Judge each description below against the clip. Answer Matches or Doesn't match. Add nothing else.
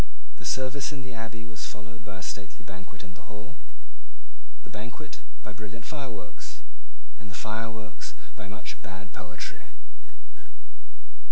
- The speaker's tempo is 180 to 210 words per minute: Doesn't match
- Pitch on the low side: Matches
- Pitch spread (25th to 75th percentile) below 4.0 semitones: Matches